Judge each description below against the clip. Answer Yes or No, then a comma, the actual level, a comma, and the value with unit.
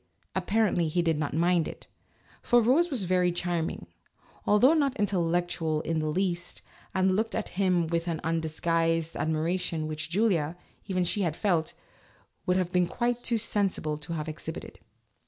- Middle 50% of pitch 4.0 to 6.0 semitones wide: No, average, 3.4 semitones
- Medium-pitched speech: Yes, medium, 175 Hz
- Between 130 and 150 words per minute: No, average, 165 wpm